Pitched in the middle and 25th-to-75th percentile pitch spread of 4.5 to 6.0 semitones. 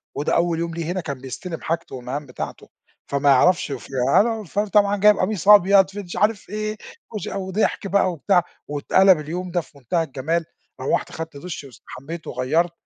Yes: medium, 175 Hz; average, 5.1 semitones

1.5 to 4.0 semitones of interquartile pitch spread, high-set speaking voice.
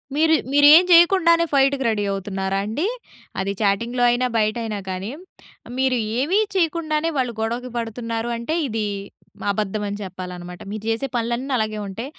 No: average, 5.1 semitones; high, 235 Hz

